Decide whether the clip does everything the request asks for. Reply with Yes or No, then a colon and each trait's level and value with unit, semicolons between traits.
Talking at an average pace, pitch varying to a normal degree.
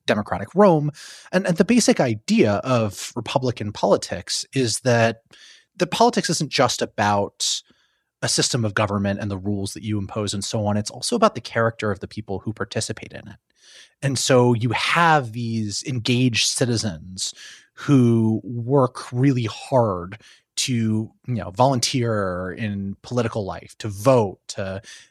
Yes: average, 150 wpm; average, 4.2 semitones